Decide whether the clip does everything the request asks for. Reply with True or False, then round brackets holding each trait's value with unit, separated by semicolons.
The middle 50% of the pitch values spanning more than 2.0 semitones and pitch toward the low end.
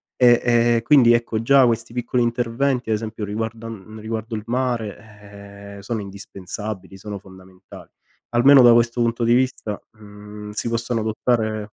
True (2.4 semitones; 115 Hz)